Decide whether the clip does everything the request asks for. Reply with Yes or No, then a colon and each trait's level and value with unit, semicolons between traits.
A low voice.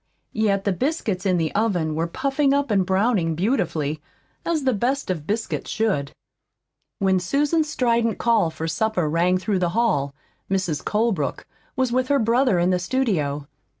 No: high, 200 Hz